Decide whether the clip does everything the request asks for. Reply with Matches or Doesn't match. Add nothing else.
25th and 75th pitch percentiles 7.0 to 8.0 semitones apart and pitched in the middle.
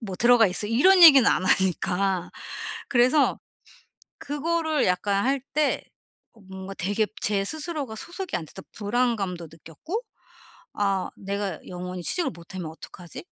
Doesn't match